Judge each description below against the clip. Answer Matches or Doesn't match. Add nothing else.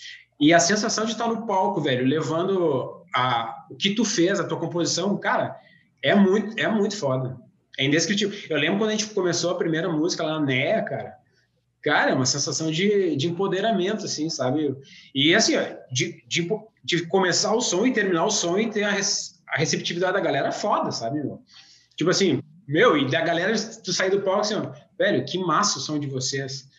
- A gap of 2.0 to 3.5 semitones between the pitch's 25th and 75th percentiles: Doesn't match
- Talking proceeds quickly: Matches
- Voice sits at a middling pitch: Matches